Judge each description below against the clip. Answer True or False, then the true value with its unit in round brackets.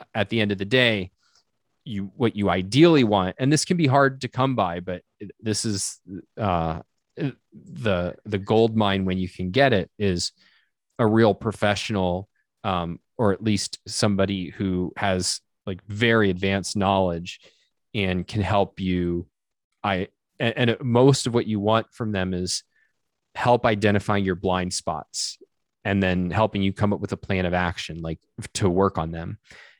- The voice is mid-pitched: False (100 Hz)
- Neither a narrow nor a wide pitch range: True (3.6 semitones)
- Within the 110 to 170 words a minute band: True (165 wpm)